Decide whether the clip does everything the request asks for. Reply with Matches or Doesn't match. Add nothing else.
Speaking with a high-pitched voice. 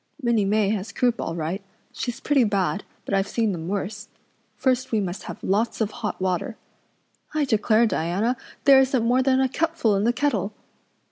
Matches